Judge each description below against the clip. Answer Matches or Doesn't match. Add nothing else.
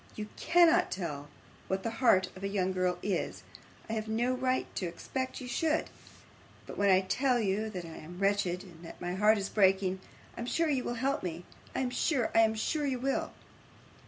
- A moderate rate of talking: Doesn't match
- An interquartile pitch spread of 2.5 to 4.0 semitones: Doesn't match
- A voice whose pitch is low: Doesn't match